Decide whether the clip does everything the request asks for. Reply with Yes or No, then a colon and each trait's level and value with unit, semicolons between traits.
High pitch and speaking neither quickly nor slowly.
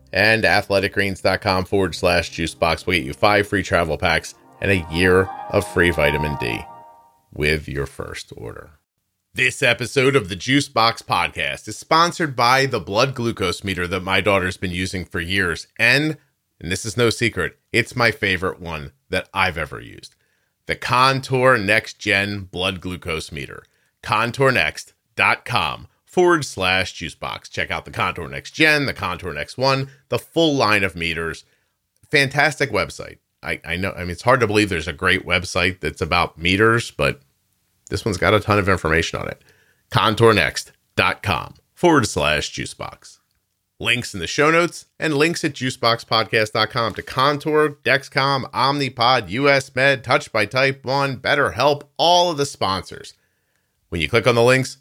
No: low, 105 Hz; average, 165 wpm